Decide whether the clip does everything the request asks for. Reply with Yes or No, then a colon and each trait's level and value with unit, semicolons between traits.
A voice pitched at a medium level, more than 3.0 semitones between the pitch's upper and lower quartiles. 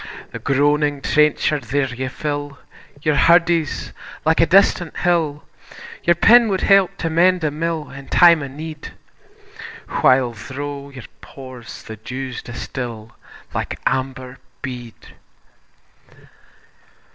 Yes: medium, 145 Hz; average, 3.9 semitones